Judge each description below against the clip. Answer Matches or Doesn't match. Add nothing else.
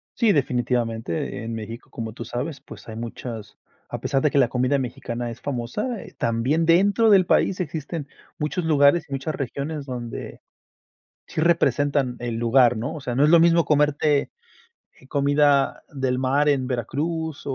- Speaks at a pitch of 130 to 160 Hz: Matches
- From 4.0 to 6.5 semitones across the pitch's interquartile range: Matches